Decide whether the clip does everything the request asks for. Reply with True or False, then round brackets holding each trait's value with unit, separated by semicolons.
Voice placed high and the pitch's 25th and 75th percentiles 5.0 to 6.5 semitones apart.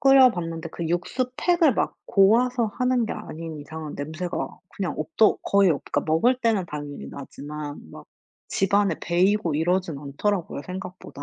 False (180 Hz; 5.6 semitones)